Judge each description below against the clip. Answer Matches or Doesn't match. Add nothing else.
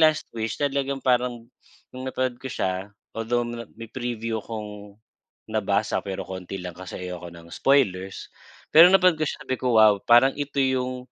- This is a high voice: Doesn't match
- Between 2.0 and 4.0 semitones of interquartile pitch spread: Doesn't match